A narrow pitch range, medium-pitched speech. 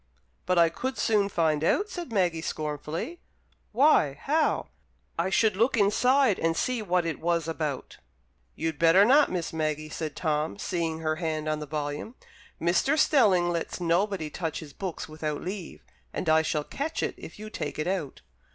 No: average, 5.0 semitones; medium, 170 Hz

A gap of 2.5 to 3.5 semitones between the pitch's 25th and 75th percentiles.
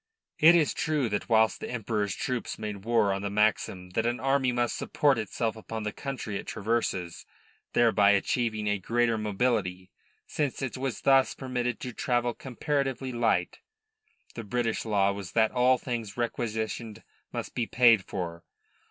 Yes: average, 3.2 semitones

